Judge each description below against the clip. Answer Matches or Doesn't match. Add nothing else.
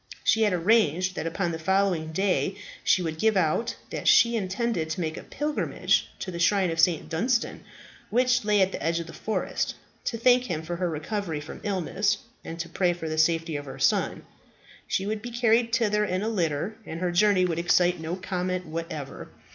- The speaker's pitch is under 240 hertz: Matches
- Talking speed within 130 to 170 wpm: Doesn't match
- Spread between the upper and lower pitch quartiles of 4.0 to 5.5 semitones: Matches